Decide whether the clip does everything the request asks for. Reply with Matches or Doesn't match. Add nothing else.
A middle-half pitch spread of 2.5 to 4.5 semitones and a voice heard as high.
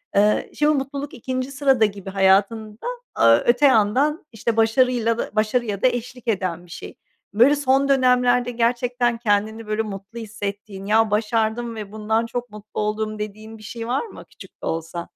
Matches